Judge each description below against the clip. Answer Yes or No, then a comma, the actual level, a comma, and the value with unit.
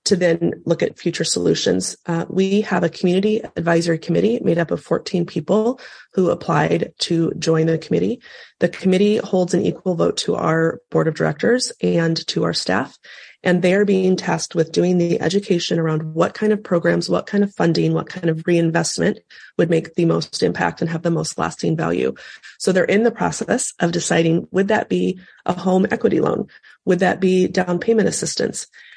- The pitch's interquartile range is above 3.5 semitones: No, average, 2.8 semitones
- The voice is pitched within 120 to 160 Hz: No, medium, 175 Hz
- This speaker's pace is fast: No, average, 190 wpm